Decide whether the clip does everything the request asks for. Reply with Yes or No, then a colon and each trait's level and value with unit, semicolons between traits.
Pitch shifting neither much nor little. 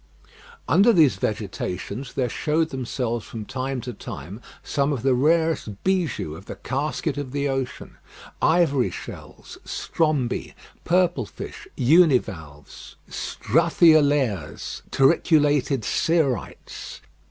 Yes: average, 4.8 semitones